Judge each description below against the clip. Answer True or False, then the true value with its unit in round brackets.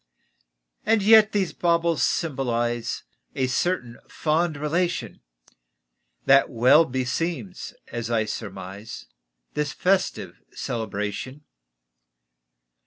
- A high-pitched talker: False (135 Hz)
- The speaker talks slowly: True (85 wpm)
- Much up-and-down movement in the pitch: True (6.4 semitones)